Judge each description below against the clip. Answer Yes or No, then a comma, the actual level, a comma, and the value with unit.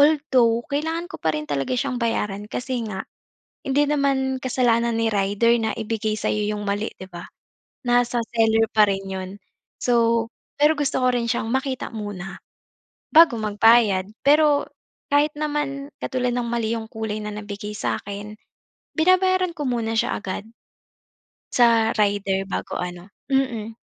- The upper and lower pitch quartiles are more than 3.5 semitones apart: Yes, average, 4.2 semitones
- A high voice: Yes, high, 230 Hz